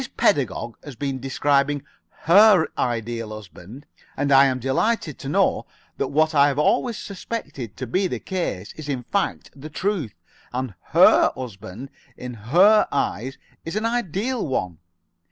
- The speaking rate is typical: Yes, average, 150 wpm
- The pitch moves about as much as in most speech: No, wide, 6.4 semitones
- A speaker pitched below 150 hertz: Yes, medium, 140 Hz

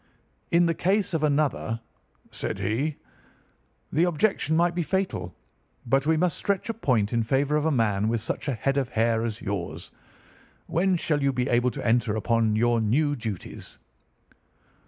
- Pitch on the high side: No, low, 135 Hz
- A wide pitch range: Yes, wide, 6.0 semitones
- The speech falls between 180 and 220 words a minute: No, average, 170 wpm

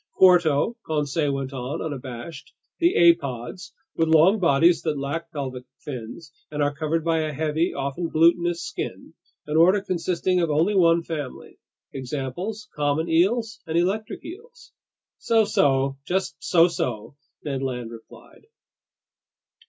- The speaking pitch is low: No, medium, 160 Hz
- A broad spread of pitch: No, average, 4.2 semitones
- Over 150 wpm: No, slow, 135 wpm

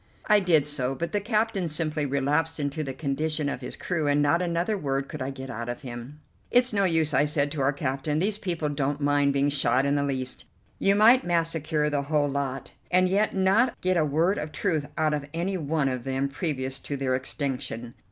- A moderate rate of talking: No, fast, 215 wpm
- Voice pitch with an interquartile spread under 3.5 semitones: No, average, 3.8 semitones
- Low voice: No, medium, 150 Hz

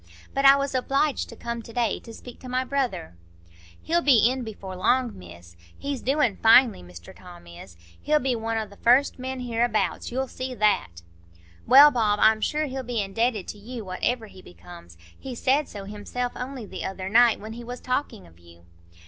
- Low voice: No, high, 235 Hz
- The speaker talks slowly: No, average, 190 wpm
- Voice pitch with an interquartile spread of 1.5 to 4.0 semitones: No, average, 4.7 semitones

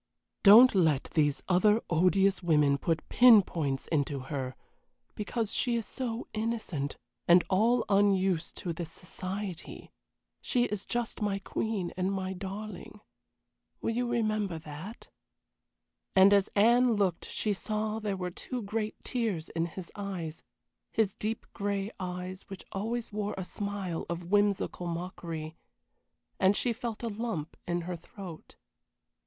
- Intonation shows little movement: No, average, 3.8 semitones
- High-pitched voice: Yes, high, 195 Hz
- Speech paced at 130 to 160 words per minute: Yes, average, 140 wpm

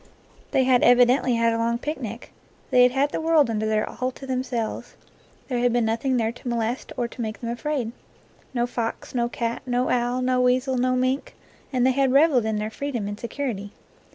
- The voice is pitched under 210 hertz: No, high, 245 Hz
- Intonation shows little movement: Yes, narrow, 1.9 semitones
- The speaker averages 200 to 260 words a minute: Yes, fast, 205 wpm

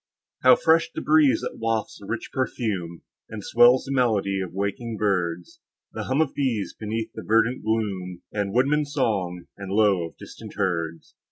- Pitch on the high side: No, low, 110 Hz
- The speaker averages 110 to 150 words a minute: No, average, 170 wpm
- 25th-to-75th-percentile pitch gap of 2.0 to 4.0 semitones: No, average, 4.5 semitones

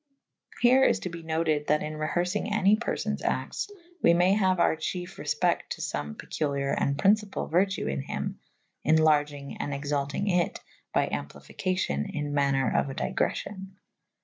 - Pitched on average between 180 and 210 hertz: No, medium, 160 Hz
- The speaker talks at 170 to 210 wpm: No, average, 160 wpm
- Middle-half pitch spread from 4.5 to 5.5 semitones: Yes, average, 4.9 semitones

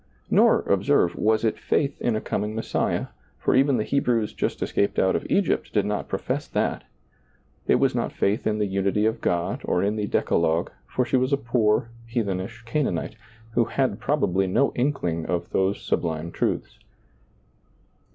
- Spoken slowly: No, average, 170 wpm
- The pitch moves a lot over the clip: No, average, 4.2 semitones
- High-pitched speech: No, low, 105 Hz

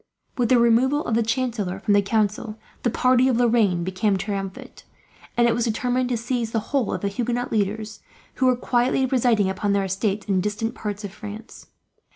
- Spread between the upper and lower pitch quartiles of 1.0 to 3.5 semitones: Yes, average, 3.2 semitones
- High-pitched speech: Yes, high, 225 Hz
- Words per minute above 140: Yes, average, 195 wpm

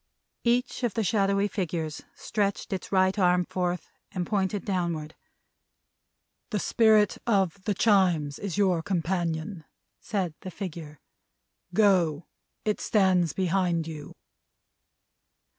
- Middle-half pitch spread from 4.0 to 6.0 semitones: No, average, 3.1 semitones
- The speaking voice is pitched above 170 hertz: Yes, medium, 185 Hz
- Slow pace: Yes, slow, 110 wpm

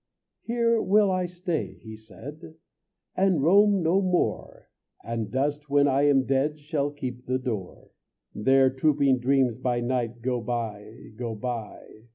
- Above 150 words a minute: No, average, 145 wpm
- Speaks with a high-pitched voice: No, low, 135 Hz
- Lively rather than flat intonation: No, average, 4.8 semitones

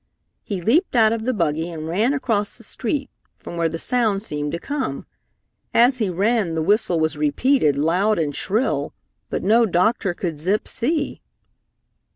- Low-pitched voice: No, high, 200 Hz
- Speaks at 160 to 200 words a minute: Yes, average, 170 wpm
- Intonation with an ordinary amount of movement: No, wide, 6.2 semitones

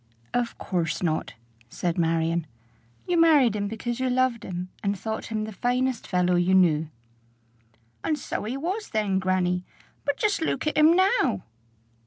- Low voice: No, high, 215 Hz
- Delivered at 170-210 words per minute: No, average, 160 wpm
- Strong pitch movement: Yes, wide, 6.4 semitones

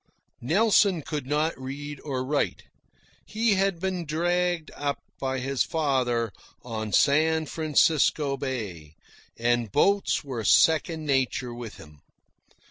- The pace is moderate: No, slow, 120 wpm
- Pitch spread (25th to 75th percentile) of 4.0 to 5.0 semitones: Yes, average, 4.4 semitones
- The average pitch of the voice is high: No, medium, 145 Hz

